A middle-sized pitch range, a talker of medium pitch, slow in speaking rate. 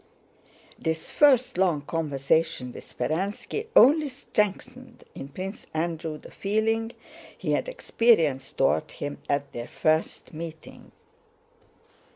No: wide, 6.8 semitones; medium, 170 Hz; slow, 110 wpm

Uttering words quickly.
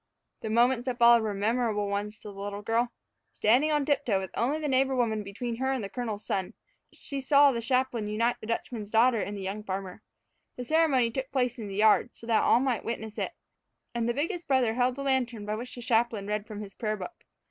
Yes: fast, 230 wpm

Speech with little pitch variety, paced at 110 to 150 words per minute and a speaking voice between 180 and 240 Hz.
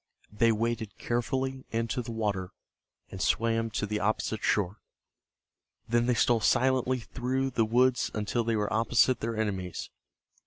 No: narrow, 2.3 semitones; average, 145 wpm; low, 115 Hz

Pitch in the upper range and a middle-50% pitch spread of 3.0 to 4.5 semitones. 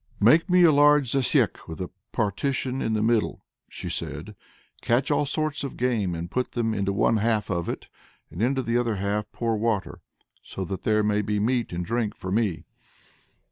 No: low, 110 Hz; average, 4.0 semitones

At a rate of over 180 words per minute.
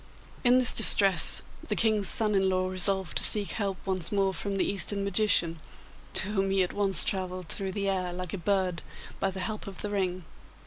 Yes: fast, 205 wpm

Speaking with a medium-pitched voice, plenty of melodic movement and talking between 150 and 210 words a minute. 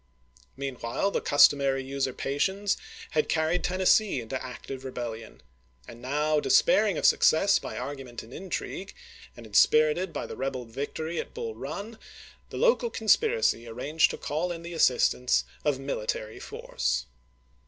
No: medium, 145 Hz; wide, 6.1 semitones; average, 140 wpm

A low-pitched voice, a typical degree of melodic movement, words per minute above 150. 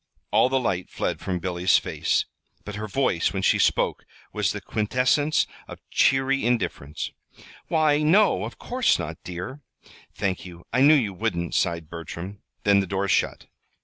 No: low, 100 Hz; wide, 7.1 semitones; average, 160 wpm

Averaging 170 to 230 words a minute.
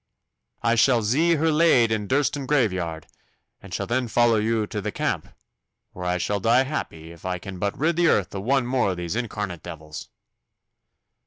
Yes: average, 185 wpm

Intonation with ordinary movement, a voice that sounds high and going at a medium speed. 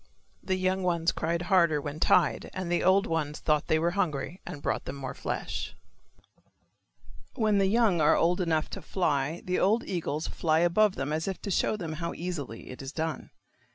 No: average, 3.3 semitones; medium, 170 Hz; average, 190 wpm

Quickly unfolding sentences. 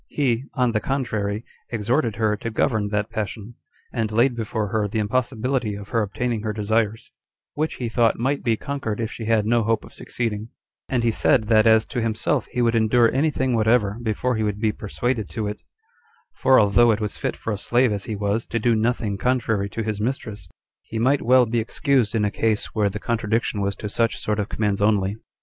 Yes: fast, 210 wpm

